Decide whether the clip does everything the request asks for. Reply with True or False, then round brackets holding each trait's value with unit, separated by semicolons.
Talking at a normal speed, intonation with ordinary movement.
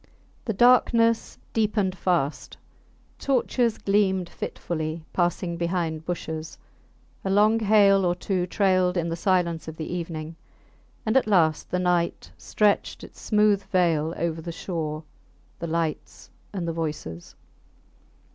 False (130 wpm; 3.5 semitones)